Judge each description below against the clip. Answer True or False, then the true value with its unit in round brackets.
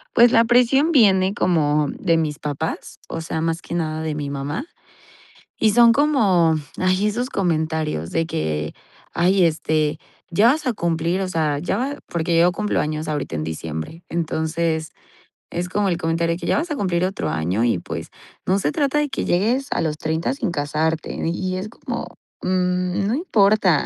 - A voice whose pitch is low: False (170 Hz)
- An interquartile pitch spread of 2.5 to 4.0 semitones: False (4.5 semitones)